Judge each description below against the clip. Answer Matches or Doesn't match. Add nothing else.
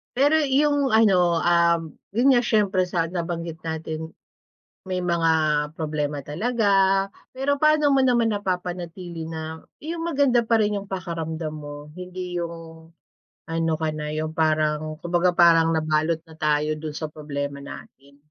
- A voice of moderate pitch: Matches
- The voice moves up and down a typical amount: Matches